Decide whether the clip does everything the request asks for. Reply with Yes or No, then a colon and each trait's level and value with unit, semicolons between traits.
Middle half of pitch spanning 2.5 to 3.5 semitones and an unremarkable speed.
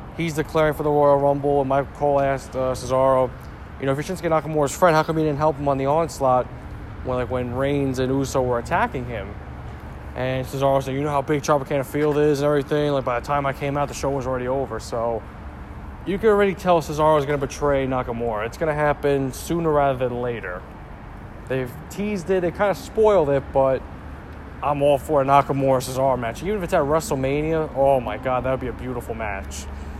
No: average, 2.9 semitones; fast, 215 wpm